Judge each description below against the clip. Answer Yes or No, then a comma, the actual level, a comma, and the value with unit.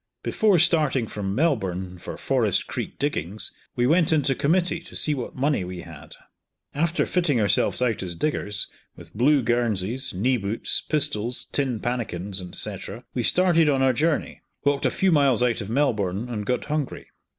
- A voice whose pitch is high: No, low, 125 Hz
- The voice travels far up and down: Yes, wide, 6.3 semitones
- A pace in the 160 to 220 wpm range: Yes, average, 165 wpm